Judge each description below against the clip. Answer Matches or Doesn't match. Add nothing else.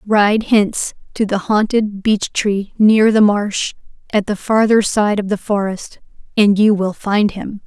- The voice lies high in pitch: Matches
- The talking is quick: Doesn't match